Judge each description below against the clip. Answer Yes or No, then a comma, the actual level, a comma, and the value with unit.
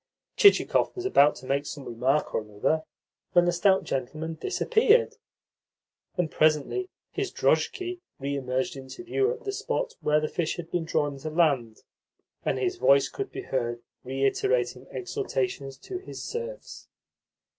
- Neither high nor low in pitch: Yes, medium, 155 Hz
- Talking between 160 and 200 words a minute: No, average, 150 wpm